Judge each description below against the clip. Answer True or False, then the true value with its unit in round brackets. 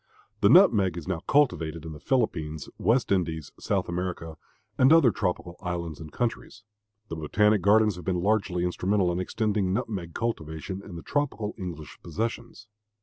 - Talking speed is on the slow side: False (155 wpm)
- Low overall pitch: True (95 Hz)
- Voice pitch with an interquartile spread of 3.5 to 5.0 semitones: True (4.5 semitones)